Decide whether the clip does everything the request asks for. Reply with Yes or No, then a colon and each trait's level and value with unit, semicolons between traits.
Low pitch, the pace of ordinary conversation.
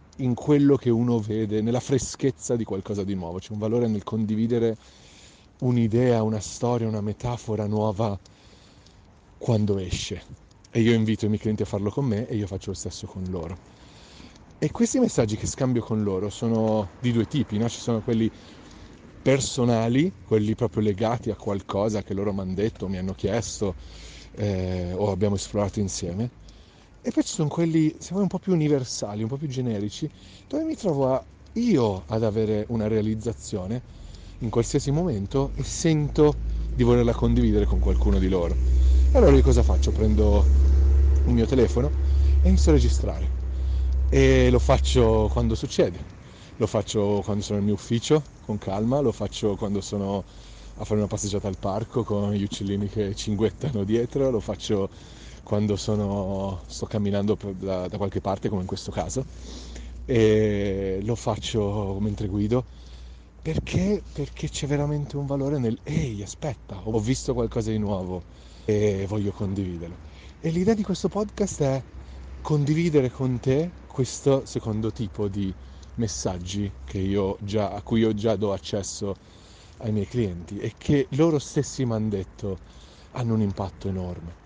Yes: low, 105 Hz; average, 160 wpm